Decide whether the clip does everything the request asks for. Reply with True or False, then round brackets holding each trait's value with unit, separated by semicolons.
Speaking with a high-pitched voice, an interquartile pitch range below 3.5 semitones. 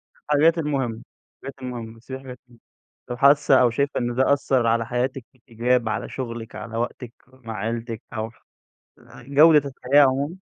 False (125 Hz; 3.0 semitones)